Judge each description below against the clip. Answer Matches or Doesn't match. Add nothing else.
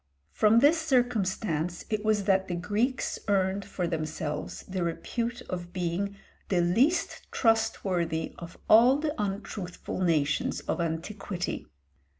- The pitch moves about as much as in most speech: Matches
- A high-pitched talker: Matches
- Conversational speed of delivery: Doesn't match